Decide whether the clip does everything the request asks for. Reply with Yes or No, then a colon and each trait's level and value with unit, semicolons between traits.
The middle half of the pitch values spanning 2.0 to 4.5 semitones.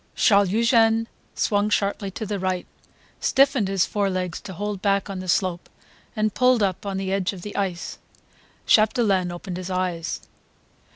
Yes: narrow, 2.4 semitones